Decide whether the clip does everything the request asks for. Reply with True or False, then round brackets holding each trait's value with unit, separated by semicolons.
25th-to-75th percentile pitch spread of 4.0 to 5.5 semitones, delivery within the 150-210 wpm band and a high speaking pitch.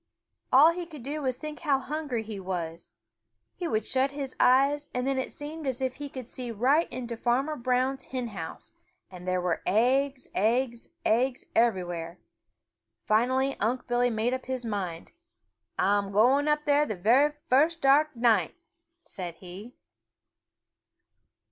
True (4.3 semitones; 155 wpm; 250 Hz)